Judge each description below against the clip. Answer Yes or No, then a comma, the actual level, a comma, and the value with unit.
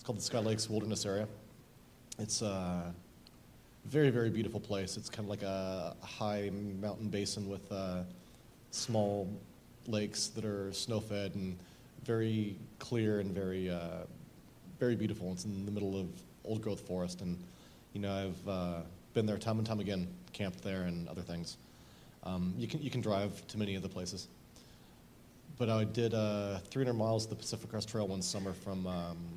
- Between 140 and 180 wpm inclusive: Yes, average, 175 wpm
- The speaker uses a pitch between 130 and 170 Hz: No, low, 100 Hz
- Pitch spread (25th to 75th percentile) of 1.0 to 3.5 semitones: Yes, average, 2.9 semitones